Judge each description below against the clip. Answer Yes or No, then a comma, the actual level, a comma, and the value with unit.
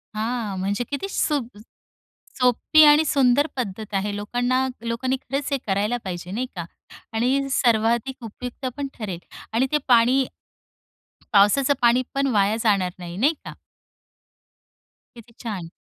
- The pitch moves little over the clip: No, average, 4.2 semitones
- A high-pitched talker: Yes, high, 235 Hz